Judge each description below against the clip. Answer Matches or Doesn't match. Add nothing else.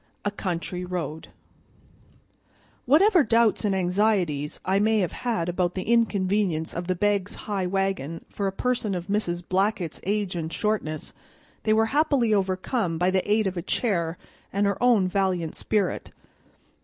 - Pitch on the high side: Matches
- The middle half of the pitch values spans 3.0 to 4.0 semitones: Matches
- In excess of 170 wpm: Doesn't match